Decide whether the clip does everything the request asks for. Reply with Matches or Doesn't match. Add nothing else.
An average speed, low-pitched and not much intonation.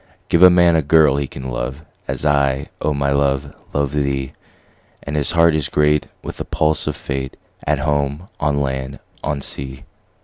Matches